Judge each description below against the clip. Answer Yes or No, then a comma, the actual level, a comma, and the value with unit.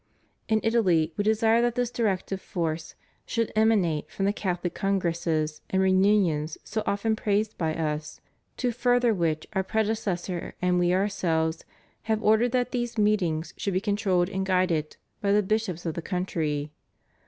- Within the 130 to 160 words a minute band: Yes, average, 155 wpm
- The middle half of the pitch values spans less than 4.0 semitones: No, average, 4.4 semitones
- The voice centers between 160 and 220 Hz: Yes, high, 190 Hz